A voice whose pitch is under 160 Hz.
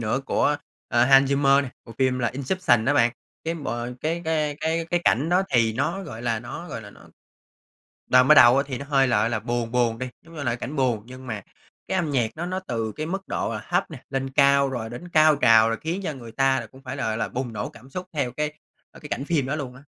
Yes: low, 135 Hz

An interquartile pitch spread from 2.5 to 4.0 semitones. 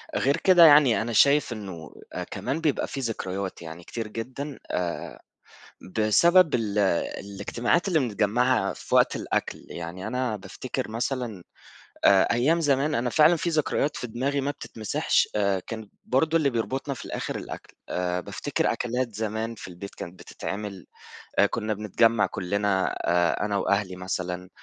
No: wide, 5.5 semitones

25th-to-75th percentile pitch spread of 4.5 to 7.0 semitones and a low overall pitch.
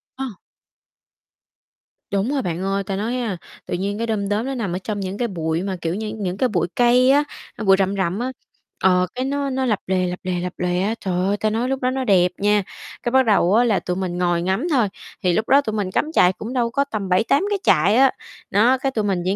No: average, 5.0 semitones; high, 205 Hz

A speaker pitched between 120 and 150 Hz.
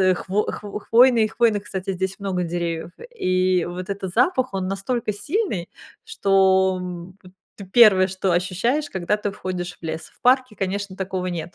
No: high, 190 Hz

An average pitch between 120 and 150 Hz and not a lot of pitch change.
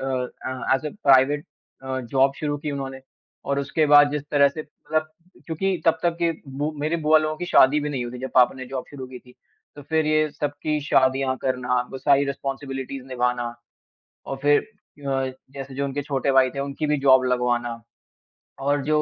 Yes: medium, 140 Hz; narrow, 2.2 semitones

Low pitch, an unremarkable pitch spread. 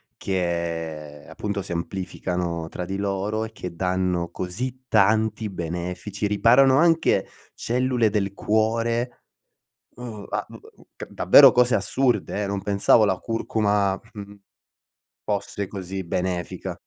Yes: low, 100 Hz; average, 3.6 semitones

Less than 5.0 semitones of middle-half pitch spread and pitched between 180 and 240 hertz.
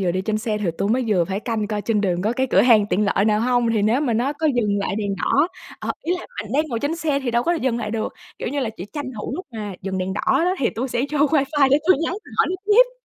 No: average, 5.3 semitones; high, 230 Hz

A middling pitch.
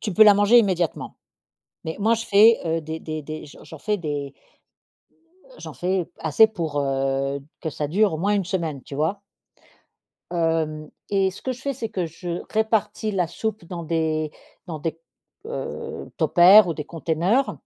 Yes: medium, 170 Hz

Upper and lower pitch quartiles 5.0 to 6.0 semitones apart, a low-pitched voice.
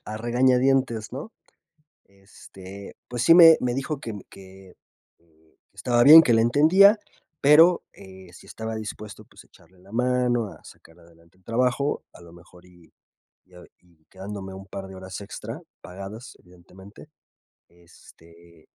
Yes: wide, 5.6 semitones; low, 100 Hz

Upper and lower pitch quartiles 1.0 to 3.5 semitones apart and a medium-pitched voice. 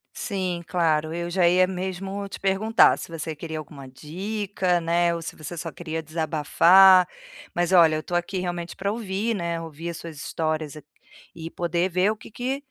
Yes: average, 2.9 semitones; medium, 175 Hz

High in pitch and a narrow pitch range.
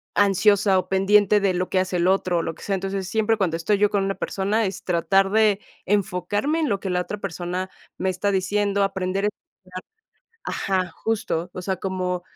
Yes: high, 195 Hz; narrow, 1.8 semitones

